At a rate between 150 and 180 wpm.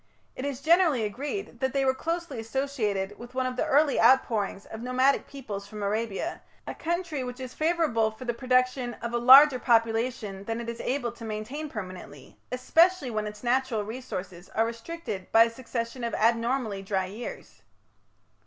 Yes: average, 170 wpm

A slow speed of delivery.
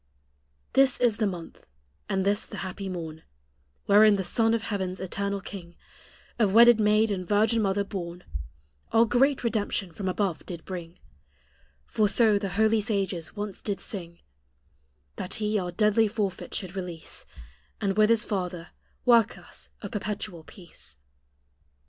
No: average, 150 wpm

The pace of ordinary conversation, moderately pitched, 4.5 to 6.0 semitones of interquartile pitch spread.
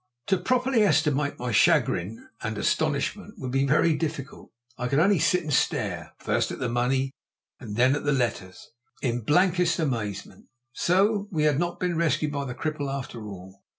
Yes: average, 175 wpm; medium, 145 Hz; wide, 5.4 semitones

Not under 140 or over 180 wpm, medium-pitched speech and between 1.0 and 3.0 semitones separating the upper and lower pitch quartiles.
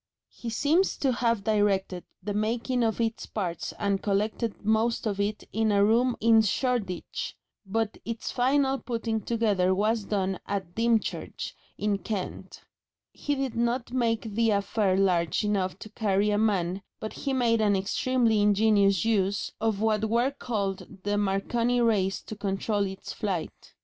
No: average, 155 wpm; high, 215 Hz; average, 2.7 semitones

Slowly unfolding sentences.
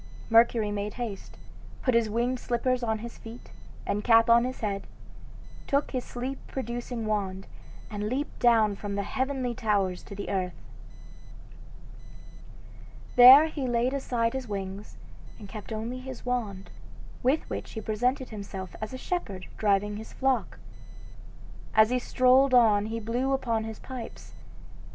No: average, 145 wpm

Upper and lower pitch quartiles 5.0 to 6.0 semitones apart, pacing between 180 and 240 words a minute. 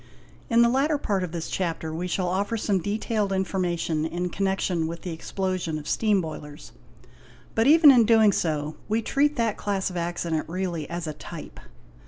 No: average, 4.5 semitones; average, 185 wpm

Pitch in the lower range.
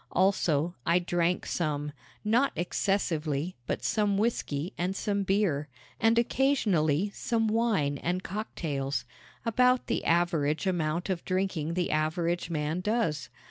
No: medium, 175 Hz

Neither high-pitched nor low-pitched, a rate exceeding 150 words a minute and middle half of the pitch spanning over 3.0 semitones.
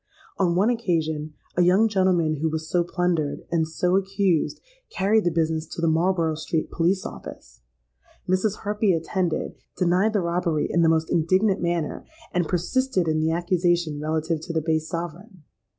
No: medium, 170 Hz; average, 165 wpm; average, 2.7 semitones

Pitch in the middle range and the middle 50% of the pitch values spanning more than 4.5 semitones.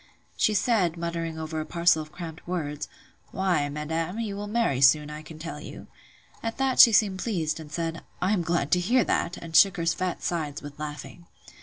No: medium, 170 Hz; average, 3.5 semitones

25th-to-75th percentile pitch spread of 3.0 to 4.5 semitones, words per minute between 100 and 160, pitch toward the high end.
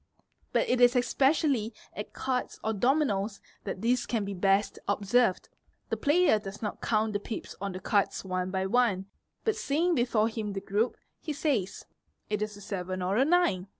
No: average, 4.2 semitones; average, 185 wpm; high, 215 Hz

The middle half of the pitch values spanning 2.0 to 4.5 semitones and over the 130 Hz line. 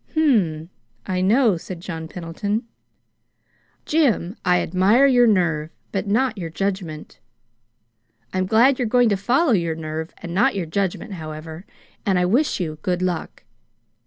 No: average, 5.1 semitones; medium, 185 Hz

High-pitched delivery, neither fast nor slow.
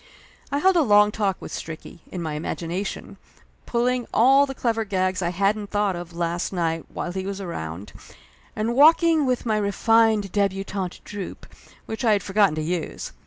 Yes: high, 200 Hz; average, 175 wpm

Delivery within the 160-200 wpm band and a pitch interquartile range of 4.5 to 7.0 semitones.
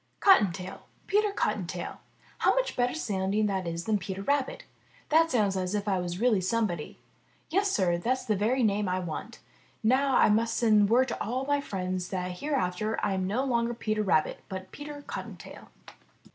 Yes: average, 175 wpm; wide, 5.4 semitones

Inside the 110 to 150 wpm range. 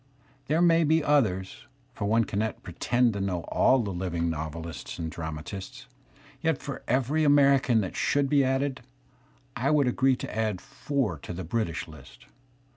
No: average, 160 wpm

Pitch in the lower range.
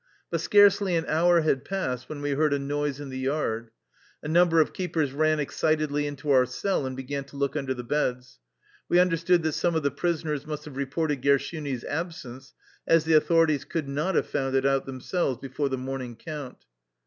No: medium, 145 Hz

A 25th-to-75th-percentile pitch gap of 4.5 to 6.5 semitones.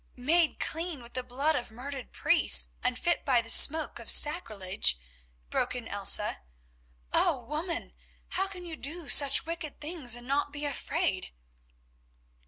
Yes: average, 5.0 semitones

